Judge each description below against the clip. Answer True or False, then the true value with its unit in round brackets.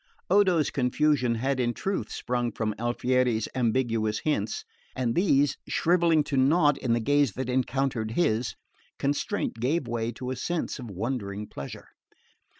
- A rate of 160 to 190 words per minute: False (145 wpm)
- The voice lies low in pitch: True (130 Hz)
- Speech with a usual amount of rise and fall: True (3.8 semitones)